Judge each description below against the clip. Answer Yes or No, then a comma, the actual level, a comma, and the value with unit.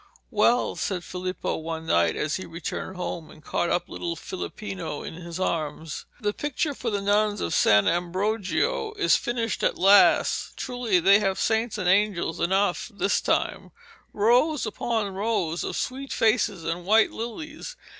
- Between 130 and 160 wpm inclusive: Yes, average, 155 wpm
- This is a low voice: No, high, 200 Hz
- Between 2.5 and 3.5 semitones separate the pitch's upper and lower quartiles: No, average, 4.6 semitones